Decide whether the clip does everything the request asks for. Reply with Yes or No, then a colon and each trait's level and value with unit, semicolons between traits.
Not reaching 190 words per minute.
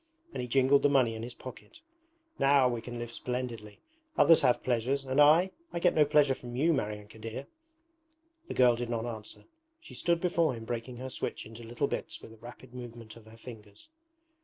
No: average, 200 wpm